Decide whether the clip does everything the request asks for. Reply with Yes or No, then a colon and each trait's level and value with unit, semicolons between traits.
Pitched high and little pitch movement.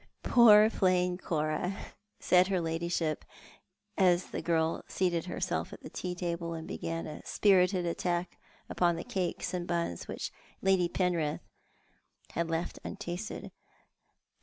No: medium, 175 Hz; narrow, 1.7 semitones